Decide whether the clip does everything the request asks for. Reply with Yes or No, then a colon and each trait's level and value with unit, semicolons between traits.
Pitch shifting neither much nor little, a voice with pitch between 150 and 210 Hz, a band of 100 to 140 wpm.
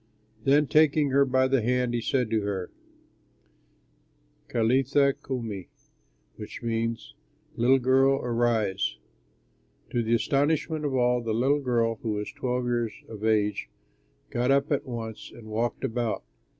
No: average, 3.1 semitones; low, 120 Hz; slow, 135 wpm